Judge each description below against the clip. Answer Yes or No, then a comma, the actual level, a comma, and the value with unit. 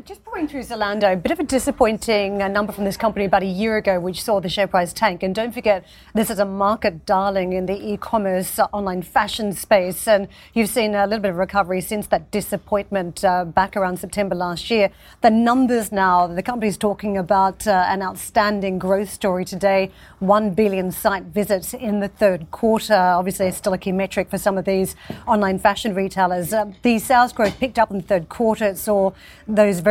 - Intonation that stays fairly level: Yes, narrow, 2.2 semitones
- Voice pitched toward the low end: No, high, 200 Hz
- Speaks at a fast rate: Yes, fast, 210 wpm